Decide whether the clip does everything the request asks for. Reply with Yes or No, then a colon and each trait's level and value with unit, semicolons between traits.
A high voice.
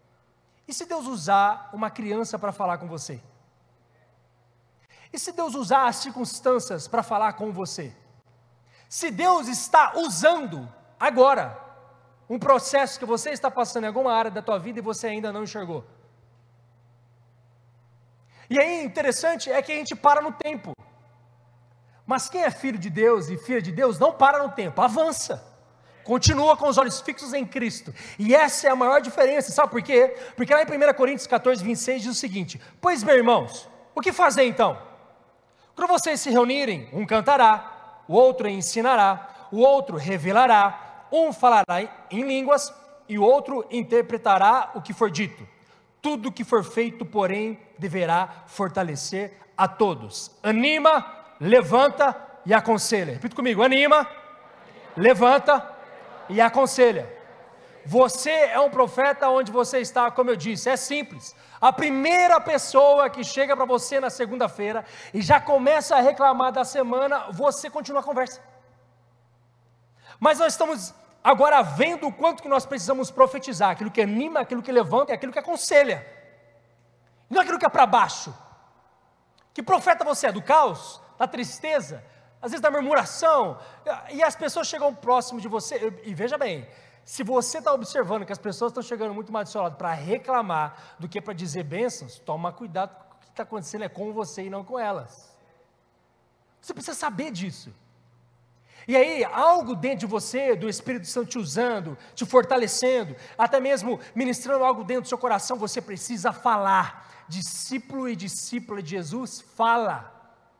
Yes: high, 240 Hz